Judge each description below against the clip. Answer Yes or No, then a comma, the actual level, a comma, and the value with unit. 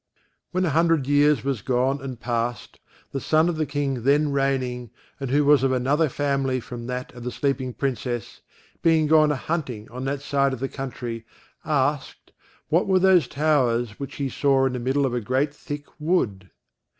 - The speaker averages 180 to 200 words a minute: Yes, average, 185 wpm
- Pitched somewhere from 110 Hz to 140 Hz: Yes, low, 135 Hz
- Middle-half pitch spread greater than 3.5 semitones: No, average, 2.8 semitones